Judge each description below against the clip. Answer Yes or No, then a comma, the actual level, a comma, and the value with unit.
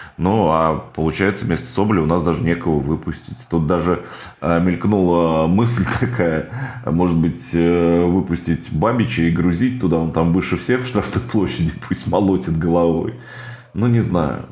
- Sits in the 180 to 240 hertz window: No, very low, 85 Hz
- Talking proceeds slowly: No, average, 145 wpm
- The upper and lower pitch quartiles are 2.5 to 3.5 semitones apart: No, average, 4.1 semitones